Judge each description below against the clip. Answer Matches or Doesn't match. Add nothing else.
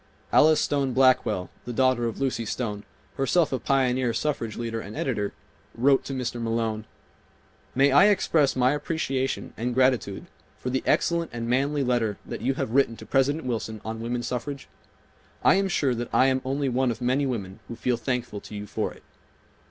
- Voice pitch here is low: Matches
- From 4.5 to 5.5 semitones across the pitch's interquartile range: Doesn't match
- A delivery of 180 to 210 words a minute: Matches